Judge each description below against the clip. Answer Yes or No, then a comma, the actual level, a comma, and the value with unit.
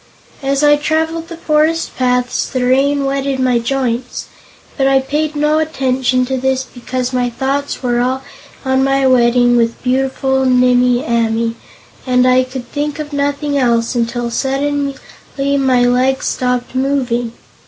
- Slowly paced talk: No, average, 145 wpm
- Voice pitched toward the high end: Yes, very high, 265 Hz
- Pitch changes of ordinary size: No, narrow, 2.1 semitones